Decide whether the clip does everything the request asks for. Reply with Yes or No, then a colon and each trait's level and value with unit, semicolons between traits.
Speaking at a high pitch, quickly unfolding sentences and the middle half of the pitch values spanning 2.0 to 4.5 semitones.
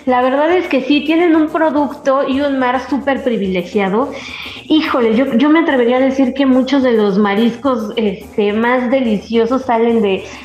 No: very high, 260 Hz; average, 170 wpm; average, 3.4 semitones